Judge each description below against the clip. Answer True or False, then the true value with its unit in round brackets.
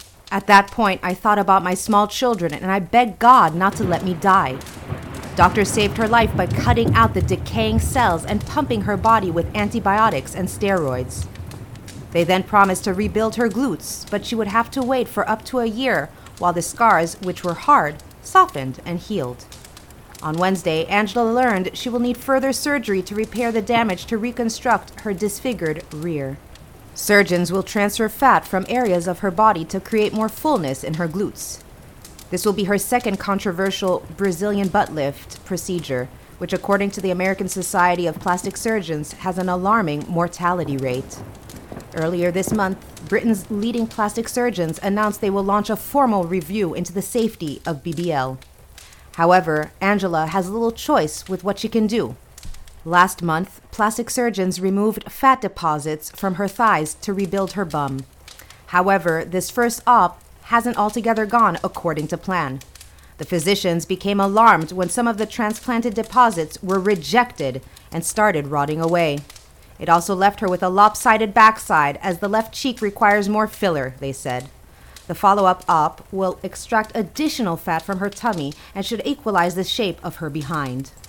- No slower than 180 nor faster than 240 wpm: False (165 wpm)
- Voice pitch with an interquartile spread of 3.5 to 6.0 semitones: True (4.6 semitones)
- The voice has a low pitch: False (195 Hz)